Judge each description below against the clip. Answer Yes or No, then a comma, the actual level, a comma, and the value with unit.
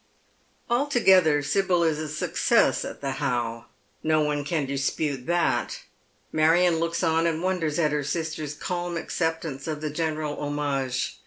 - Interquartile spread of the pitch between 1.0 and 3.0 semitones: Yes, narrow, 2.4 semitones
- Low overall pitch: No, medium, 155 Hz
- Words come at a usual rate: Yes, average, 150 wpm